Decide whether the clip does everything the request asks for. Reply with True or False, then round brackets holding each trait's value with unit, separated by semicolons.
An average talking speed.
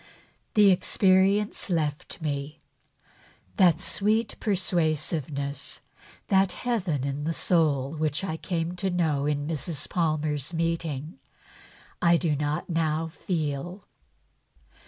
False (110 wpm)